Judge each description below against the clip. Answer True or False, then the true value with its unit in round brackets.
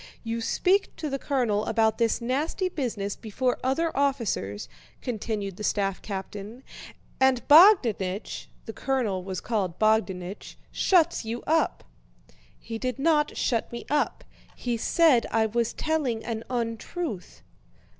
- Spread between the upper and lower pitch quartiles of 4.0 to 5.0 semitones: True (4.4 semitones)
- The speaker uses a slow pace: True (130 wpm)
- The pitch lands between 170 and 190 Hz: False (235 Hz)